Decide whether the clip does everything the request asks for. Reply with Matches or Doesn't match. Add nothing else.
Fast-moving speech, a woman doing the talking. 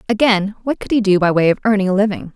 Matches